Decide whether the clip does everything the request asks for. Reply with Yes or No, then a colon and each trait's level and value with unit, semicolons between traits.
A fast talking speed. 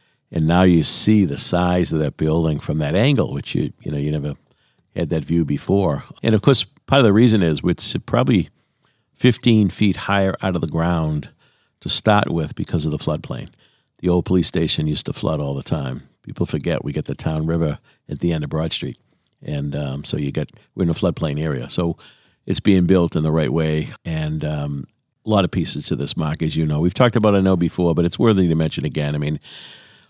Yes: fast, 225 wpm